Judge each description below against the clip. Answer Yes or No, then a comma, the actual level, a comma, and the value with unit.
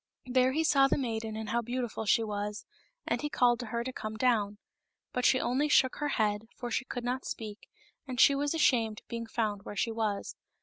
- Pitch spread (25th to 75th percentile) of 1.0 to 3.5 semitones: Yes, average, 2.9 semitones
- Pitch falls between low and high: No, high, 235 Hz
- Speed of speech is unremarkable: No, fast, 220 wpm